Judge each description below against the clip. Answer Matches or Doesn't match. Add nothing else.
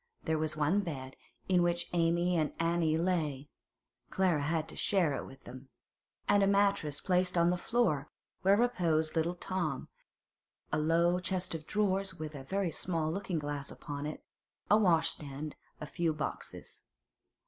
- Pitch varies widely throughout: Doesn't match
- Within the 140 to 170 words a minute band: Matches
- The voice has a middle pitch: Matches